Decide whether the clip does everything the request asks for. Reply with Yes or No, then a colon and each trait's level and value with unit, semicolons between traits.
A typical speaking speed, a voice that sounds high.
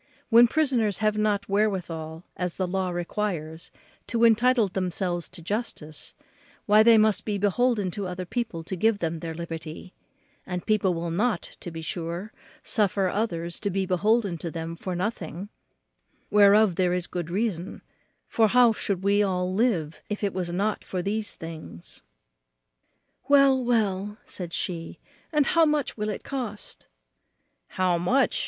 Yes: average, 155 wpm; high, 195 Hz